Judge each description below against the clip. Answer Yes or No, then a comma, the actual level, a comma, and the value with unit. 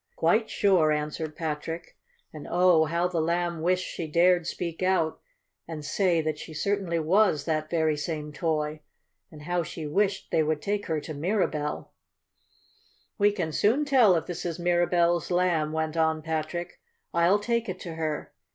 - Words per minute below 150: No, average, 165 wpm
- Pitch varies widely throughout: No, narrow, 2.6 semitones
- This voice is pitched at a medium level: Yes, medium, 170 Hz